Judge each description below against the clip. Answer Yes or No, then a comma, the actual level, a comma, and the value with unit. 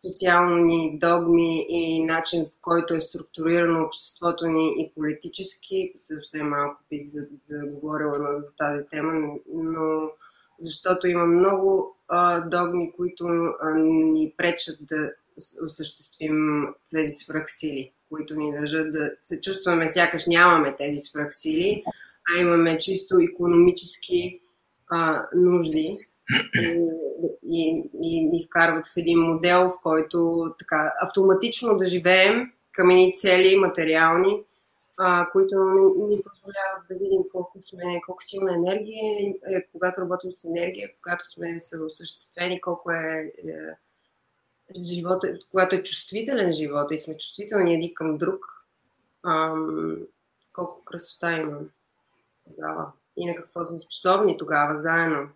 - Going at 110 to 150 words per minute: Yes, average, 125 wpm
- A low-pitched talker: No, medium, 170 Hz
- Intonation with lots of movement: No, average, 2.7 semitones